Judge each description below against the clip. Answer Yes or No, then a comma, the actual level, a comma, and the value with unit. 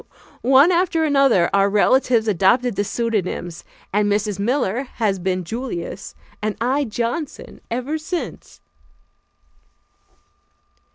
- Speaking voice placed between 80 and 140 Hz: No, high, 230 Hz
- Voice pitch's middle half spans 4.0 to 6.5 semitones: Yes, average, 5.1 semitones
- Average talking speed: No, slow, 105 wpm